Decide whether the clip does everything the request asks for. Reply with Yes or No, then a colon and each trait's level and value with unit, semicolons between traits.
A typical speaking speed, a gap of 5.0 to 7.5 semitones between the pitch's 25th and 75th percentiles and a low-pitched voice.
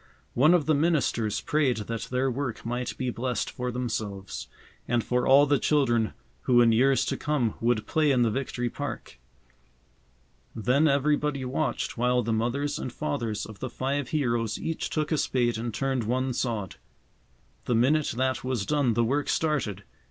No: average, 170 wpm; average, 3.4 semitones; low, 125 Hz